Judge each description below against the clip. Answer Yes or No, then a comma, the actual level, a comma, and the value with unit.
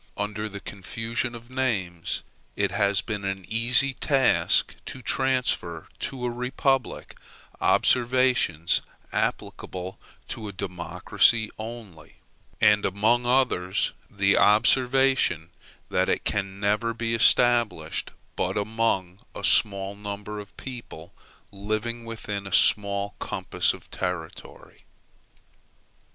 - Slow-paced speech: Yes, slow, 110 wpm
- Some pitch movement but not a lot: Yes, average, 3.6 semitones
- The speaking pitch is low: Yes, low, 105 Hz